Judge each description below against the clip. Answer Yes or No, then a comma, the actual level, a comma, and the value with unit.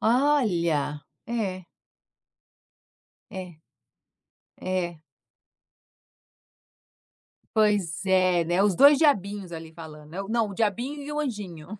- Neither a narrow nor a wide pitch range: Yes, average, 5.0 semitones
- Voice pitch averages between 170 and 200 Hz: Yes, high, 190 Hz